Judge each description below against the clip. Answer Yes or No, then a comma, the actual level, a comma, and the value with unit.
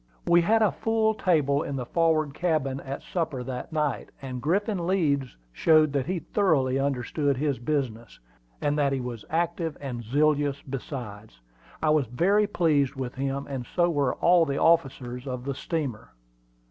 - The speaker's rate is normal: Yes, average, 170 wpm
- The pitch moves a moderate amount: Yes, average, 4.1 semitones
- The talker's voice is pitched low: No, medium, 145 Hz